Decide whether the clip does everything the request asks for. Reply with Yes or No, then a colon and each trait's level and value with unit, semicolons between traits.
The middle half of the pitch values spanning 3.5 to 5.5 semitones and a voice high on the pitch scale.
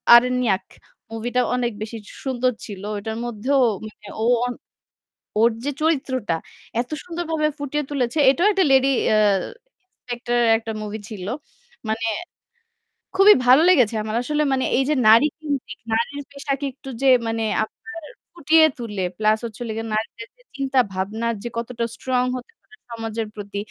Yes: average, 3.9 semitones; high, 245 Hz